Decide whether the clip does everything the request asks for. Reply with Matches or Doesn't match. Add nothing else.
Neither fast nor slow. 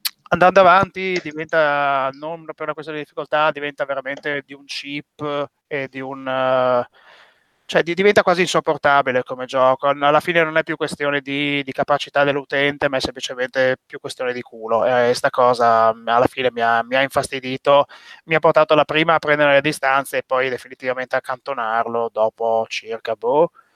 Doesn't match